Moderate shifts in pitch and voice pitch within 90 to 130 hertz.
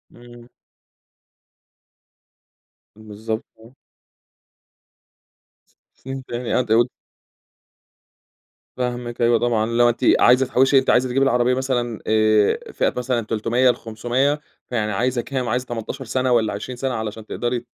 No: narrow, 2.2 semitones; low, 120 Hz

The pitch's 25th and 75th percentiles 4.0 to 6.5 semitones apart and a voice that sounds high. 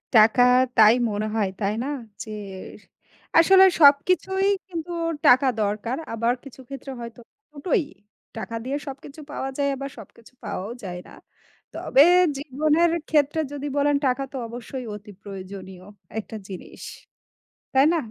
Yes: average, 5.1 semitones; very high, 260 Hz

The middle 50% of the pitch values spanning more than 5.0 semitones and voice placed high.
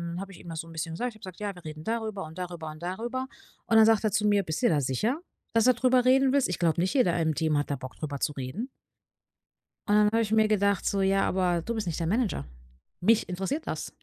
Yes: wide, 5.4 semitones; high, 195 Hz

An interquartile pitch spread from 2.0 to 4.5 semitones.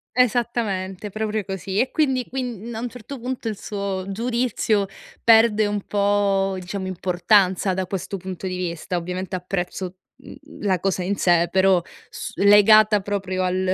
Yes: average, 2.7 semitones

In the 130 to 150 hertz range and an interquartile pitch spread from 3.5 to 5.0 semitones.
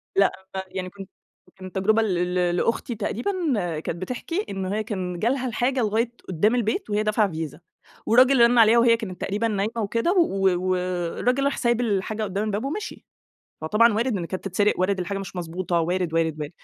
No: high, 205 Hz; average, 4.1 semitones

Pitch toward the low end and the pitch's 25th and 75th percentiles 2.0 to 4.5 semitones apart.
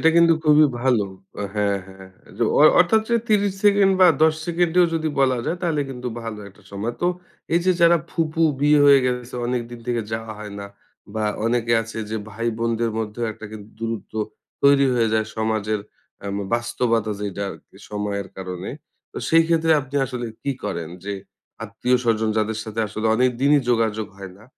No: low, 115 Hz; average, 5.3 semitones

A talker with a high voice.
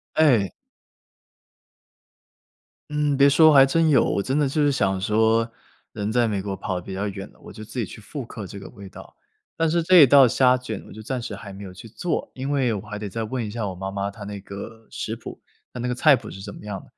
No: low, 110 Hz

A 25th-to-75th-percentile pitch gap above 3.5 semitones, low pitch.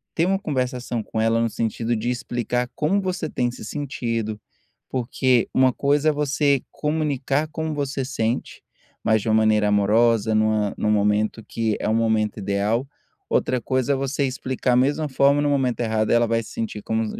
Yes: average, 4.1 semitones; low, 120 Hz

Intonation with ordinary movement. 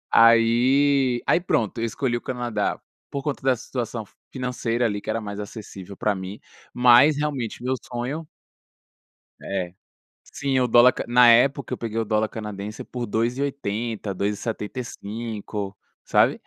Yes: average, 3.1 semitones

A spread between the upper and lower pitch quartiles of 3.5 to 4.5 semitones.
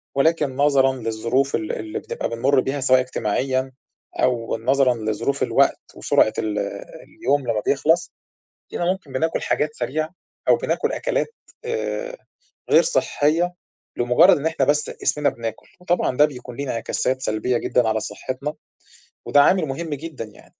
Yes: average, 3.9 semitones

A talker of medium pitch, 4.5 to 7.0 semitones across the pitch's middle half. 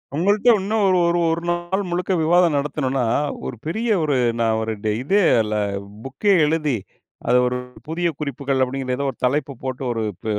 Yes: medium, 150 Hz; average, 5.0 semitones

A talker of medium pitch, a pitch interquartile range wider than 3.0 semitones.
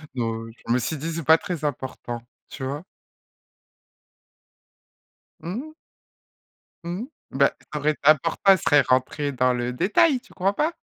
Yes: medium, 150 Hz; wide, 5.4 semitones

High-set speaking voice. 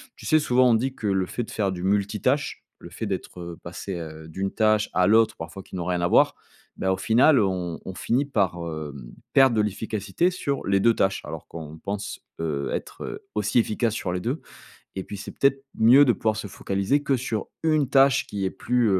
No: low, 105 Hz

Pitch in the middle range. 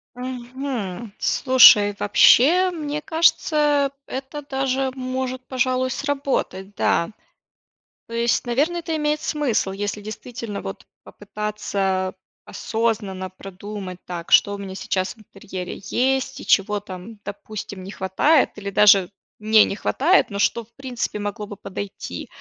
No: high, 225 Hz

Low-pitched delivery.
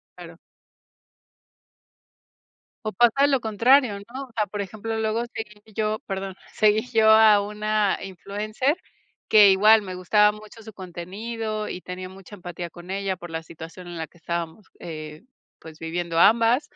No: high, 205 Hz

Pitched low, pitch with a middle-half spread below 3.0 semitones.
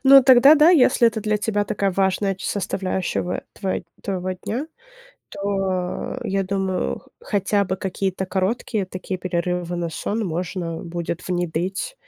No: high, 190 Hz; narrow, 2.6 semitones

